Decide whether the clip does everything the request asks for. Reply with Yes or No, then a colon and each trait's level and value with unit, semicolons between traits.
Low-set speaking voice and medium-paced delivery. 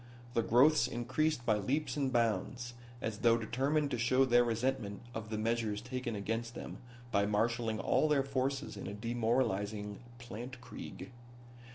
Yes: low, 120 Hz; average, 150 wpm